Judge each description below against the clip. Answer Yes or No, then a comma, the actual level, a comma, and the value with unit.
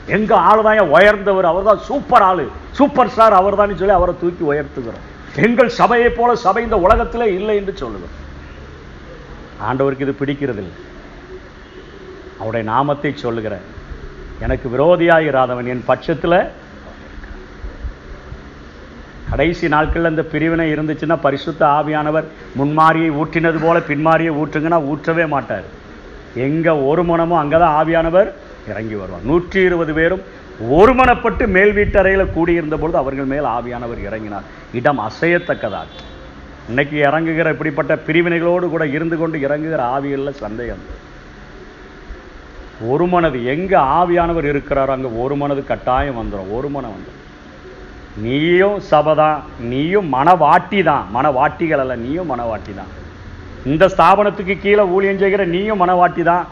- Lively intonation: Yes, wide, 8.1 semitones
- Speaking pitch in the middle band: Yes, medium, 150 Hz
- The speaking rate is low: No, average, 115 wpm